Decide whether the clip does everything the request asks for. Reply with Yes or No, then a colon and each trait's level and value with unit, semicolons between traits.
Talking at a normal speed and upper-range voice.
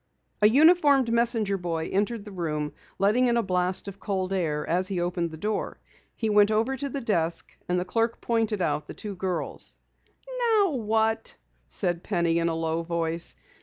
Yes: average, 180 wpm; high, 200 Hz